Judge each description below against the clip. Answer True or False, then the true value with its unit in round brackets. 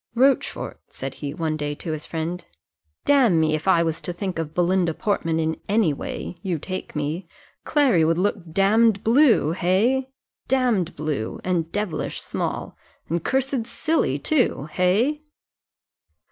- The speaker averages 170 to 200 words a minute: False (145 wpm)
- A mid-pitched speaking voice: True (180 Hz)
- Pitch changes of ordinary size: False (6.0 semitones)